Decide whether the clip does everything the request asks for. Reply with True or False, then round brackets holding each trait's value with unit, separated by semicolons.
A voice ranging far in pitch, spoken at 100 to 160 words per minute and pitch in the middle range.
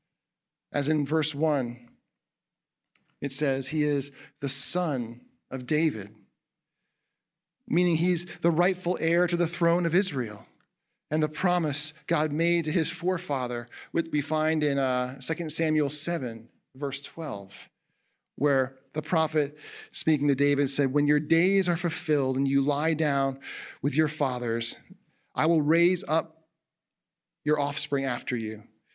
False (3.1 semitones; 140 wpm; 150 Hz)